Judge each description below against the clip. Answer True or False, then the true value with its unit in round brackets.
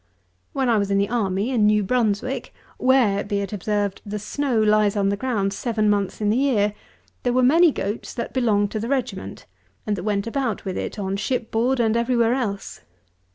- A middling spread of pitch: True (3.4 semitones)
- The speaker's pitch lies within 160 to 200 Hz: False (215 Hz)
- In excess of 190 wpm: True (200 wpm)